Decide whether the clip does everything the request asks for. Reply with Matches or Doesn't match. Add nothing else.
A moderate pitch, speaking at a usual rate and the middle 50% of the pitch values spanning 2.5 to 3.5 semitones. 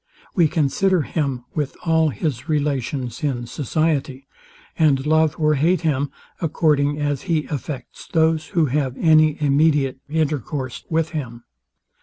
Doesn't match